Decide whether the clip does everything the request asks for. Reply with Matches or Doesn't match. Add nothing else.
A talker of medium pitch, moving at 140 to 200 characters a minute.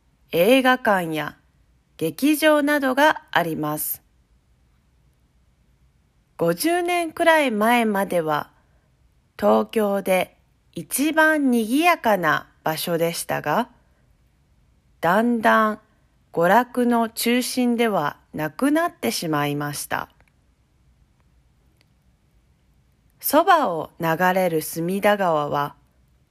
Matches